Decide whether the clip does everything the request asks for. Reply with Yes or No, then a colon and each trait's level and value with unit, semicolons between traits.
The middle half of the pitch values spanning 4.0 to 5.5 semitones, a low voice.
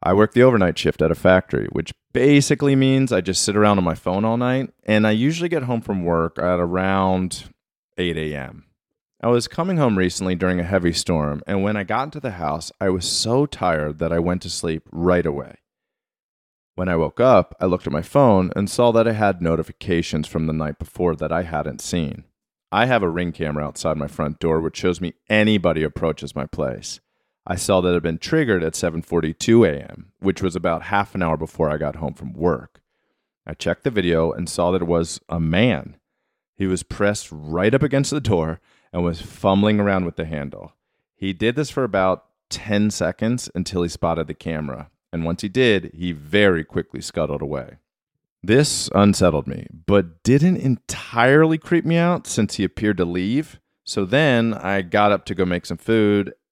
Yes: average, 4.5 semitones; very low, 90 Hz